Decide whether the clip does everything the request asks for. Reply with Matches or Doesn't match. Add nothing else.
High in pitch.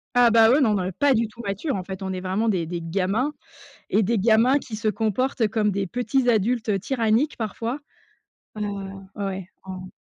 Matches